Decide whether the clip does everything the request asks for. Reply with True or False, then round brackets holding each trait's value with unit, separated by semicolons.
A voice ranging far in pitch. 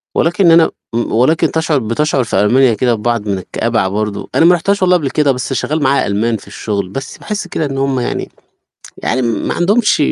True (6.2 semitones)